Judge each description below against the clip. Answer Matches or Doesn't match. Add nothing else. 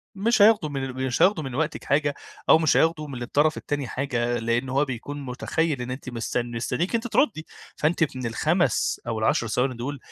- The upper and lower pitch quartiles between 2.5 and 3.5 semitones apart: Doesn't match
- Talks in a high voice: Doesn't match